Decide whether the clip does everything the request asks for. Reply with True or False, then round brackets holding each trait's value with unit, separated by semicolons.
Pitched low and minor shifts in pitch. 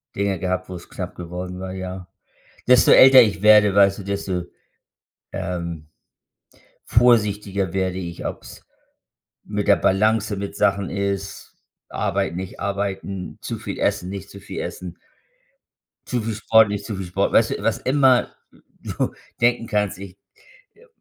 True (100 Hz; 2.2 semitones)